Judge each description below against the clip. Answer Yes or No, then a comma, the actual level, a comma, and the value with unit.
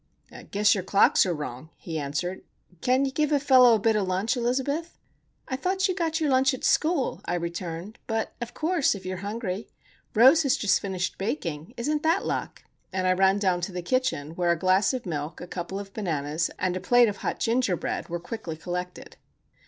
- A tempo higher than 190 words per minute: Yes, fast, 205 wpm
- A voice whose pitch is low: No, high, 200 Hz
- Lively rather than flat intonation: Yes, wide, 6.4 semitones